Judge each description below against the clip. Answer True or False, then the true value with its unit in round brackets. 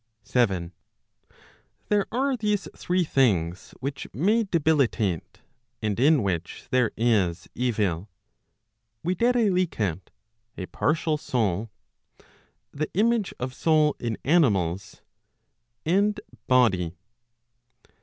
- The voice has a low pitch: True (130 Hz)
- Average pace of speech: False (90 wpm)